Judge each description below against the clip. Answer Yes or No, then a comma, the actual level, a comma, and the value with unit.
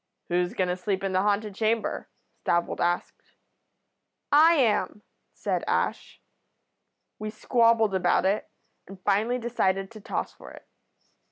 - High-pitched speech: Yes, high, 205 Hz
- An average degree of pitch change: Yes, average, 3.3 semitones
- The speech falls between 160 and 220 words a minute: No, slow, 135 wpm